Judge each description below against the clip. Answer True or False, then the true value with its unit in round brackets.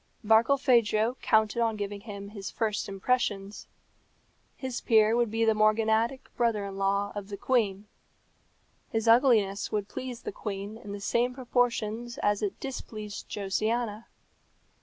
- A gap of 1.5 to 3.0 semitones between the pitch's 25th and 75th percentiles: True (2.6 semitones)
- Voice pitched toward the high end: True (215 Hz)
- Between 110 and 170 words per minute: True (140 wpm)